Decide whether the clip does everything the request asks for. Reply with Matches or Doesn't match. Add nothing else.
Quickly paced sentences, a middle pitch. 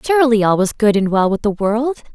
Doesn't match